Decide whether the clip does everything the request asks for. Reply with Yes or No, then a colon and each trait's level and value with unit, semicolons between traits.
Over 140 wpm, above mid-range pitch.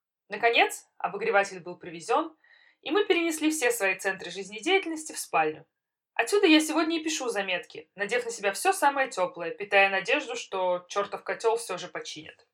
Yes: fast, 160 wpm; high, 215 Hz